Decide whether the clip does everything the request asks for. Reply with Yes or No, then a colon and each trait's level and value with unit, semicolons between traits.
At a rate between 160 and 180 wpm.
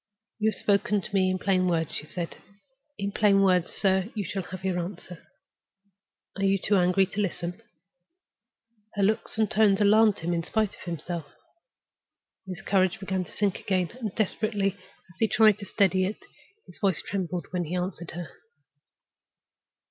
Yes: average, 170 wpm